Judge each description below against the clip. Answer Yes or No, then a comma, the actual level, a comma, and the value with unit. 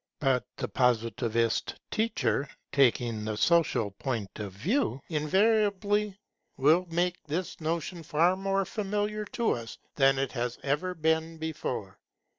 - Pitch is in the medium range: Yes, medium, 160 Hz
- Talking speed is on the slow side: Yes, slow, 125 wpm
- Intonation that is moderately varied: No, wide, 7.3 semitones